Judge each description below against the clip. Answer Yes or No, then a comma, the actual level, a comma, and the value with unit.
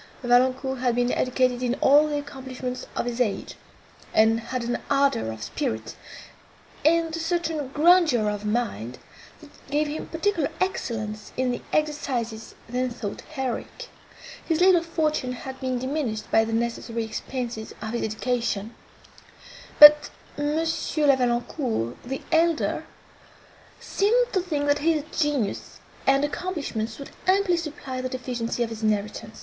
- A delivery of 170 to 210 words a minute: No, average, 140 wpm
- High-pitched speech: Yes, very high, 255 Hz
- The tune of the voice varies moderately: Yes, average, 4.6 semitones